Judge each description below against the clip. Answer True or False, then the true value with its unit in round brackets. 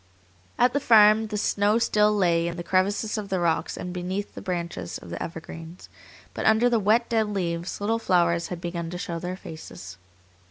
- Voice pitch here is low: False (185 Hz)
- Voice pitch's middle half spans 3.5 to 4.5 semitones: True (3.8 semitones)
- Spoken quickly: False (195 wpm)